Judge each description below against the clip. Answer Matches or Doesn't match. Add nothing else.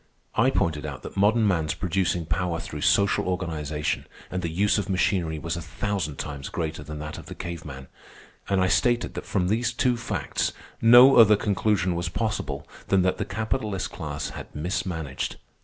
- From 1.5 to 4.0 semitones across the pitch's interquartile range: Doesn't match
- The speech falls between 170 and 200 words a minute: Matches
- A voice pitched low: Matches